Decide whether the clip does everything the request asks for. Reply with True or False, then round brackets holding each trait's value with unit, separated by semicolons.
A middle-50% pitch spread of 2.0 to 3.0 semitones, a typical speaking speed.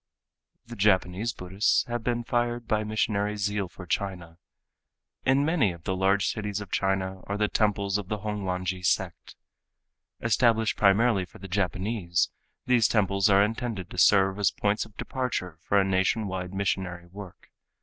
True (2.5 semitones; 160 wpm)